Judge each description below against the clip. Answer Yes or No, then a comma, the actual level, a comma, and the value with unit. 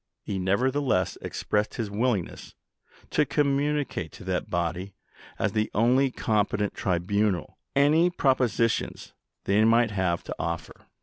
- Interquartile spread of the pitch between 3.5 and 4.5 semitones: No, wide, 5.5 semitones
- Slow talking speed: Yes, slow, 120 wpm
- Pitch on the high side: No, low, 110 Hz